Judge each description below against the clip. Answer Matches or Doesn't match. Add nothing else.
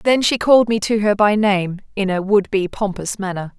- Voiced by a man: Doesn't match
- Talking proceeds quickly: Matches